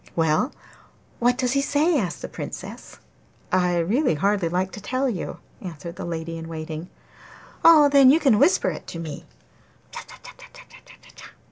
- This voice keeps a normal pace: Yes, average, 145 wpm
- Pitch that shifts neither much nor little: No, wide, 7.8 semitones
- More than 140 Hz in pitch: Yes, high, 190 Hz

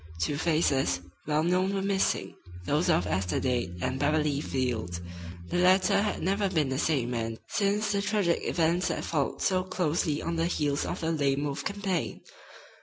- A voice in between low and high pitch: Yes, medium, 155 Hz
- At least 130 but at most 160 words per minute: No, average, 175 wpm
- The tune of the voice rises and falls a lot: Yes, wide, 5.7 semitones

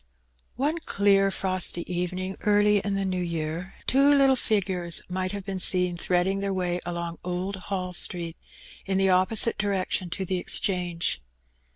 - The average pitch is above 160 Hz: Yes, medium, 185 Hz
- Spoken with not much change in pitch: Yes, narrow, 1.9 semitones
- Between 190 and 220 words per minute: No, average, 155 wpm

